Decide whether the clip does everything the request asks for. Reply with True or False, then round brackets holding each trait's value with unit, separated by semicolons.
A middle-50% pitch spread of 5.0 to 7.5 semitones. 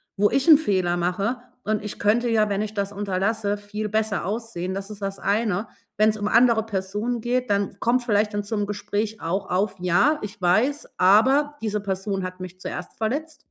False (2.4 semitones)